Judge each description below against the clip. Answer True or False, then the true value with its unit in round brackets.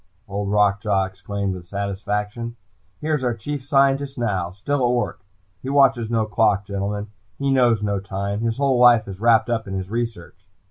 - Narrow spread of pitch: False (3.5 semitones)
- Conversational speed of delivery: True (185 wpm)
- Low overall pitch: True (110 Hz)